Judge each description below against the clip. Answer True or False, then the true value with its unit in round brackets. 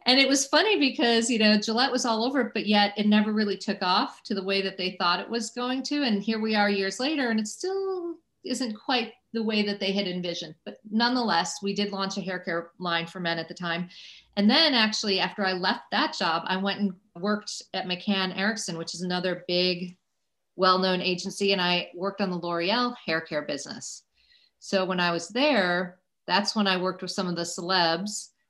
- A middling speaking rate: False (220 wpm)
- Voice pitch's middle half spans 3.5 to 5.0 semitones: True (3.9 semitones)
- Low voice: False (200 Hz)